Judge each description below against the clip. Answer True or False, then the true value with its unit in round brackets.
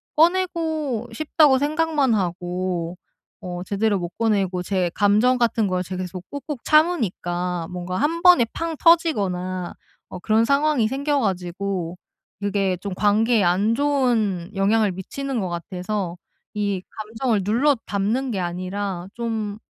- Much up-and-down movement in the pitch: True (6.4 semitones)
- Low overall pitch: False (205 Hz)